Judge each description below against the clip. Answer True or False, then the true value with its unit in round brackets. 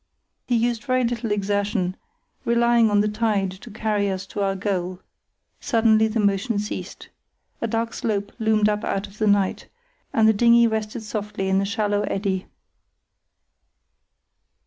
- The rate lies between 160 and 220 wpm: False (150 wpm)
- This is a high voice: True (210 Hz)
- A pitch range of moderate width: False (2.2 semitones)